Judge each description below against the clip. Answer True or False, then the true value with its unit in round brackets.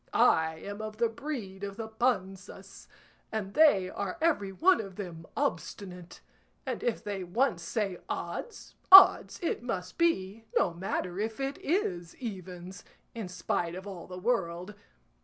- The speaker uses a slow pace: False (150 wpm)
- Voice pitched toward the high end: True (200 Hz)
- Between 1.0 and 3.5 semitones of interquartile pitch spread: False (4.6 semitones)